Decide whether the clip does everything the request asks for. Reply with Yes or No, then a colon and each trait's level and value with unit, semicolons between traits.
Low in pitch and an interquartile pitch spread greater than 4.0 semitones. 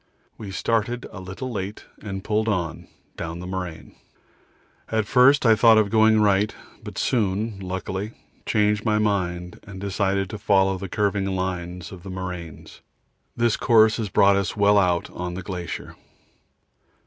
No: low, 100 Hz; narrow, 2.6 semitones